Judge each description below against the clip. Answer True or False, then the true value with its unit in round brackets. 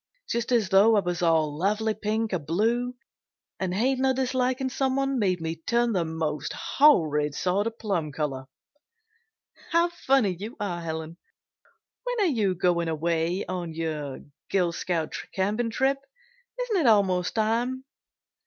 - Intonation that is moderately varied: False (6.5 semitones)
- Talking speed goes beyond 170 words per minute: False (145 wpm)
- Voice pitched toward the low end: False (195 Hz)